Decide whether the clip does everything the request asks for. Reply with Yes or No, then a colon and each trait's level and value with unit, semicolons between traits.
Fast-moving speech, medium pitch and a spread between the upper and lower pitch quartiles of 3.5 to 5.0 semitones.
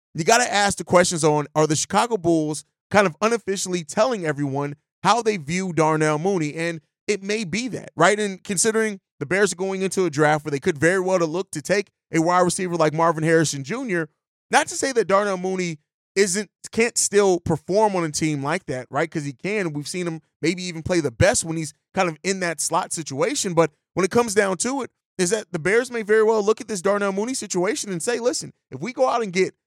Yes: fast, 235 wpm; medium, 180 Hz; average, 4.3 semitones